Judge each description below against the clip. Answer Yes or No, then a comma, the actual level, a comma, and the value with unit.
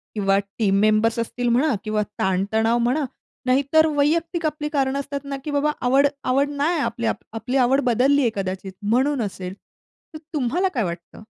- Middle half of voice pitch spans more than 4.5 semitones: Yes, average, 5.0 semitones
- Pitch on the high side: Yes, very high, 255 Hz